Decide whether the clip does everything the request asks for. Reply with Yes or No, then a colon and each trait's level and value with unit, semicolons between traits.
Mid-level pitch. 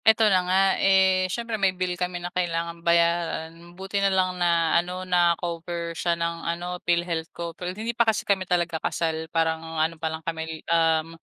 Yes: medium, 170 Hz